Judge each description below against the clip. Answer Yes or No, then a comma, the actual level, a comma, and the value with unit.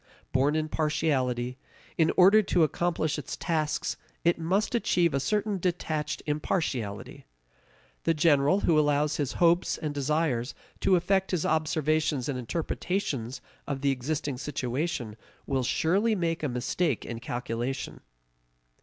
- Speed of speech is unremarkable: No, slow, 130 wpm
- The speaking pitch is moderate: Yes, medium, 150 Hz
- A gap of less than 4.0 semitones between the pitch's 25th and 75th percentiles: No, average, 4.3 semitones